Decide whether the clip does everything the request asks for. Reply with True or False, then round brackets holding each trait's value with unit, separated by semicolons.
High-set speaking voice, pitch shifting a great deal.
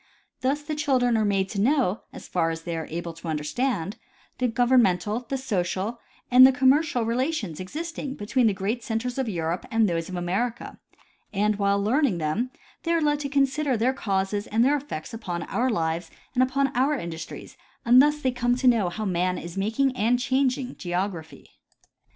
True (230 Hz; 6.0 semitones)